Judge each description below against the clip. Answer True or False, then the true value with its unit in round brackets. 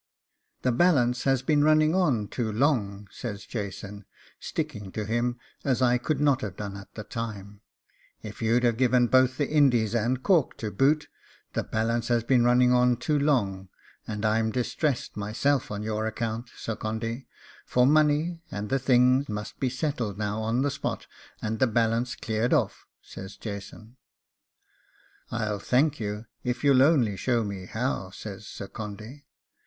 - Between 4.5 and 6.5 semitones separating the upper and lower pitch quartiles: False (3.6 semitones)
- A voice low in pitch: True (120 Hz)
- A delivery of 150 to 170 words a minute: True (165 wpm)